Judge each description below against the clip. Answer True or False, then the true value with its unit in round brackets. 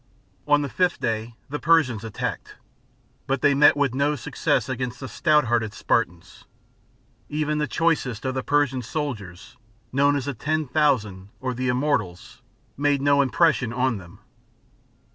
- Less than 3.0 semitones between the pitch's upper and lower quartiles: False (3.9 semitones)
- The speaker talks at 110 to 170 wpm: True (150 wpm)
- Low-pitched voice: True (130 Hz)